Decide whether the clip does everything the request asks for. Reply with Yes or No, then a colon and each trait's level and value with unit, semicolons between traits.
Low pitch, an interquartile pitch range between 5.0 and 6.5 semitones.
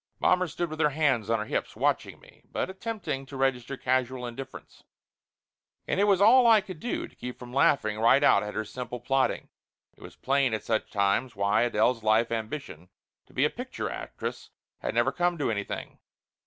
Yes: low, 130 Hz; wide, 5.5 semitones